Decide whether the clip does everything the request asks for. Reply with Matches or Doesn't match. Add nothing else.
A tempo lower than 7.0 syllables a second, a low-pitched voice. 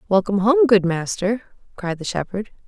Doesn't match